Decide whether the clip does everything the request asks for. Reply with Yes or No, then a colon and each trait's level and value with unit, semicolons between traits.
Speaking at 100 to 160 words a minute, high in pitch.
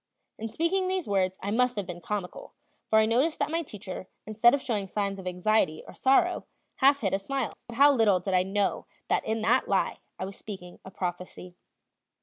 No: fast, 205 wpm; high, 210 Hz